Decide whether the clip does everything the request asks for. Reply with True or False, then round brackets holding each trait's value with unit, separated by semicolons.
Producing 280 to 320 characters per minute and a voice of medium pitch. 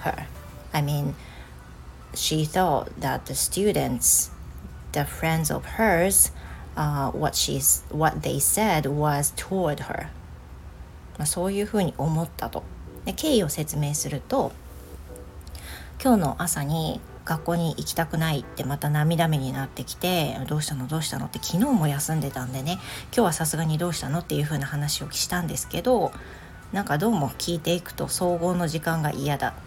True (285 characters per minute; 150 Hz)